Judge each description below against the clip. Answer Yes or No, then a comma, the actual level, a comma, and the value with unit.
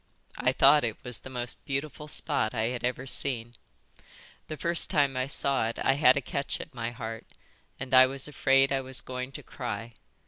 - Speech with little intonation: Yes, narrow, 2.3 semitones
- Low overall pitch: Yes, low, 130 Hz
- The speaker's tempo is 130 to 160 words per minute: No, average, 200 wpm